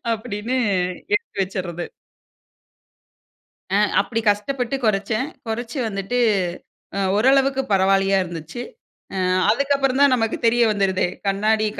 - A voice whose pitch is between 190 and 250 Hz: Yes, high, 220 Hz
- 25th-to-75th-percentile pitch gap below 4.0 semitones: No, average, 4.5 semitones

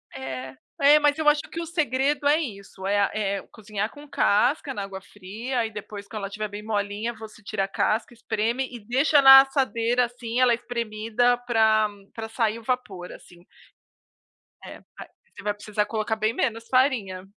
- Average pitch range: Yes, average, 3.7 semitones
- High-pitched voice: Yes, high, 225 Hz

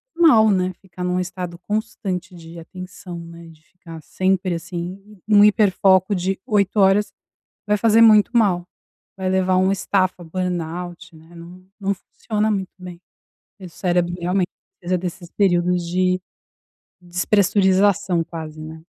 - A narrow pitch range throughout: Yes, narrow, 2.2 semitones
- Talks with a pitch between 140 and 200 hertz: Yes, medium, 185 Hz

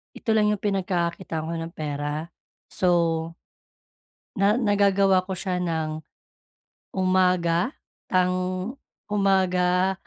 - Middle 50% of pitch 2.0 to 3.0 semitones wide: Yes, narrow, 2.4 semitones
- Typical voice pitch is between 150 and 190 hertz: Yes, medium, 185 Hz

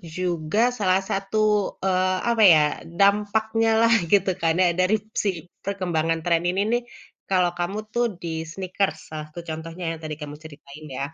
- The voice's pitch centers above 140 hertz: Yes, medium, 185 Hz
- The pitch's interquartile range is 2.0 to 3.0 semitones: No, average, 3.6 semitones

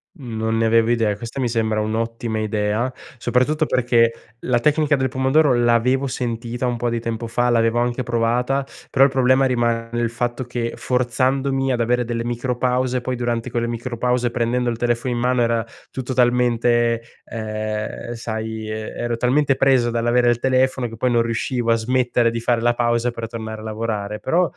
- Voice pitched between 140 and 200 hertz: No, low, 120 Hz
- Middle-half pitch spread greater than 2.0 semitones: No, narrow, 1.6 semitones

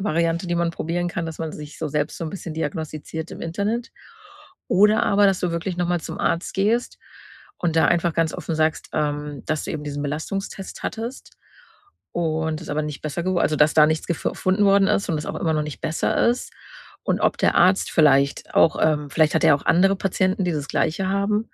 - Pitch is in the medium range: Yes, medium, 165 Hz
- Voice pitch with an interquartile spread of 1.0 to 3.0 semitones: No, average, 3.5 semitones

